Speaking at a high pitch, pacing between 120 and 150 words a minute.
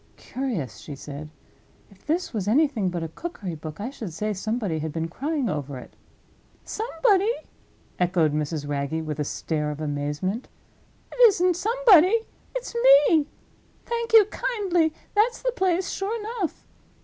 Yes: high, 240 Hz; average, 145 wpm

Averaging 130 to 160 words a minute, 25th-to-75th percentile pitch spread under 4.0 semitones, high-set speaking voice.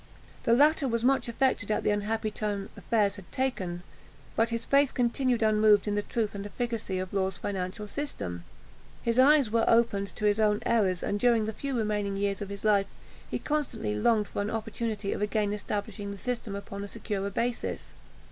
No: average, 190 wpm; narrow, 2.6 semitones; high, 210 Hz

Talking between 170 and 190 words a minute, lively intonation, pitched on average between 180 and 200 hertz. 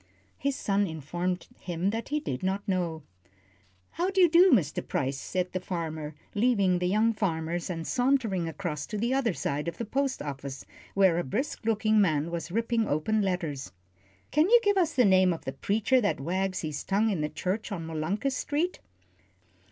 Yes: average, 185 wpm; wide, 5.8 semitones; high, 190 Hz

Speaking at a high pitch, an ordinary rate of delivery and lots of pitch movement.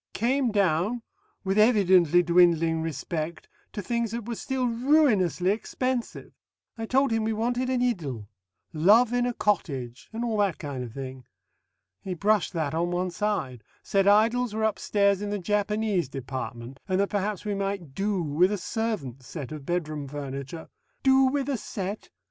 Yes: high, 195 Hz; average, 165 wpm; wide, 5.9 semitones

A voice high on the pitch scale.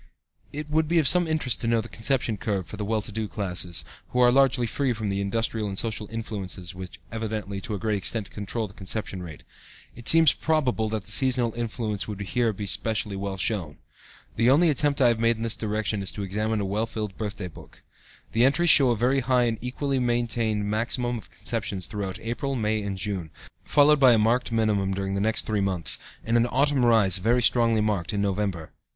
No: low, 110 Hz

